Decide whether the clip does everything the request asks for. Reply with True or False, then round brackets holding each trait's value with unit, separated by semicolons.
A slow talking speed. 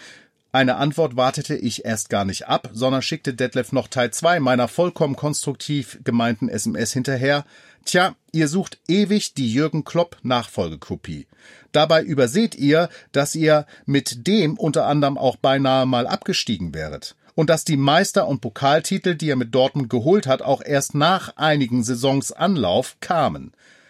False (155 wpm)